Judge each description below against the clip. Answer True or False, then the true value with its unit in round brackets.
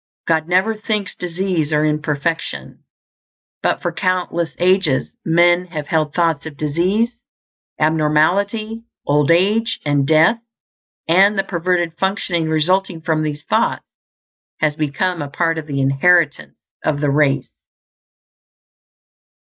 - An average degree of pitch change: True (3.4 semitones)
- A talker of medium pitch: True (165 Hz)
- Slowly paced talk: True (120 wpm)